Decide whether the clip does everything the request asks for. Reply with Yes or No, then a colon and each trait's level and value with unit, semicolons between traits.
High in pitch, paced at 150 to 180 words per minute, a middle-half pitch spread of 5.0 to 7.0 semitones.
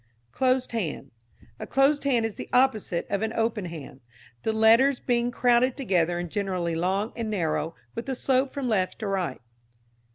Yes: high, 220 Hz; average, 170 wpm; wide, 5.6 semitones